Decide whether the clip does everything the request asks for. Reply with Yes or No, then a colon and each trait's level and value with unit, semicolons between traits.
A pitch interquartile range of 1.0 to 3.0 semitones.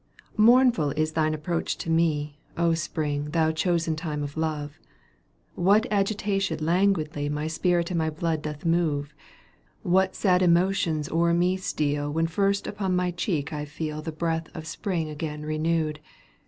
Yes: average, 2.7 semitones